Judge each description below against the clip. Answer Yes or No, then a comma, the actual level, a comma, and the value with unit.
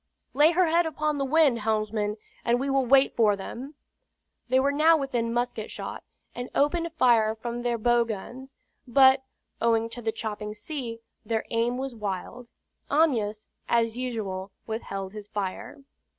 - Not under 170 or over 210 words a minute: No, average, 155 wpm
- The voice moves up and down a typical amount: Yes, average, 3.8 semitones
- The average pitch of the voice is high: Yes, high, 240 Hz